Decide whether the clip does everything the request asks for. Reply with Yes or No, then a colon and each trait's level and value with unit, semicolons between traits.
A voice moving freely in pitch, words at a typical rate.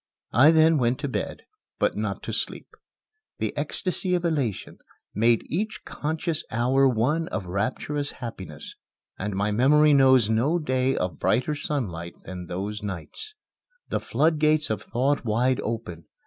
Yes: wide, 6.1 semitones; average, 145 wpm